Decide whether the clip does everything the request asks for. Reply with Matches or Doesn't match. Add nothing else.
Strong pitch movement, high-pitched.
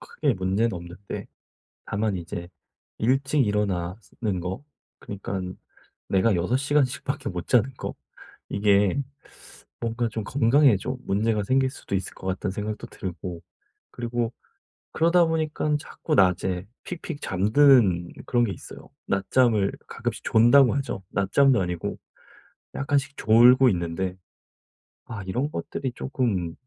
Doesn't match